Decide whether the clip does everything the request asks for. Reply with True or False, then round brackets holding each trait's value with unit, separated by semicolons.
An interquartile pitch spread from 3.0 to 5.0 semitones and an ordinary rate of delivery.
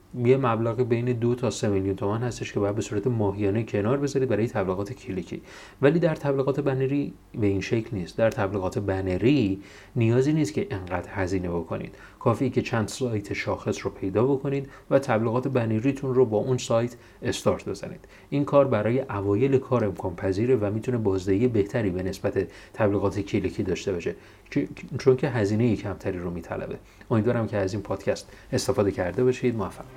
False (4.3 semitones; 170 wpm)